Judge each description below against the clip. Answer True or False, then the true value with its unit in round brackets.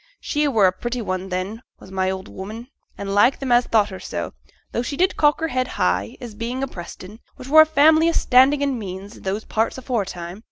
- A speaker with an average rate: False (230 wpm)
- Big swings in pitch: True (5.7 semitones)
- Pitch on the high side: True (225 Hz)